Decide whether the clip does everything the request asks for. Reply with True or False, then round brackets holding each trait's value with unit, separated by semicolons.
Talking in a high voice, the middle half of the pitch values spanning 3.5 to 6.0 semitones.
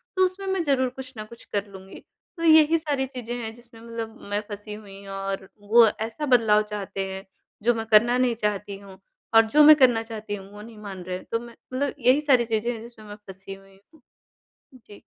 True (225 Hz; 3.8 semitones)